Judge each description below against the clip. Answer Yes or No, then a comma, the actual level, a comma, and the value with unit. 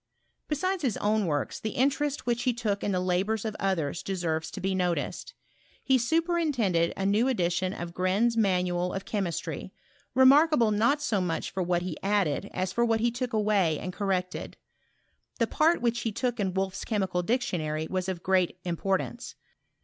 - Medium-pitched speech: No, high, 200 Hz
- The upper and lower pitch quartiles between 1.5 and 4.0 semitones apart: No, average, 4.7 semitones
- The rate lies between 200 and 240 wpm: No, average, 170 wpm